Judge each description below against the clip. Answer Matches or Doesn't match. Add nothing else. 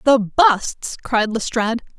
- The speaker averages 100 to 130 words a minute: Matches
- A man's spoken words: Doesn't match